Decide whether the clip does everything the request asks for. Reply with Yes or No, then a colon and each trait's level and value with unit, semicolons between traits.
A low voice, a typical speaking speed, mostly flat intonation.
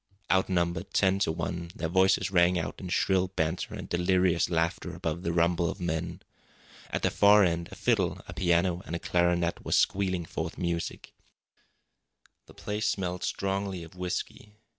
Yes: very low, 90 Hz; average, 160 wpm; narrow, 1.8 semitones